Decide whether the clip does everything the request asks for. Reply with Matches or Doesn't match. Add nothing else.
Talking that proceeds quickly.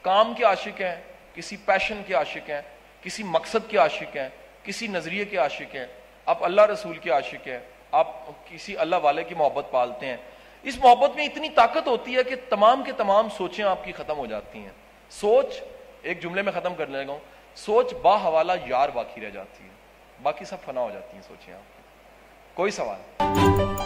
Doesn't match